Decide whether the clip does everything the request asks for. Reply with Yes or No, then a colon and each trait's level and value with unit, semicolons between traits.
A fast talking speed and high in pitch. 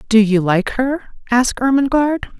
No: average, 150 wpm; high, 245 Hz